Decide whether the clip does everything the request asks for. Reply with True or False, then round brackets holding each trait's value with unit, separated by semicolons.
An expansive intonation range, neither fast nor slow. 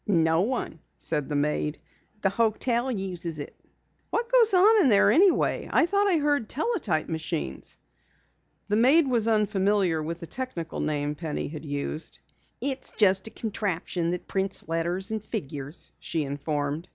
True (7.2 semitones; 150 wpm)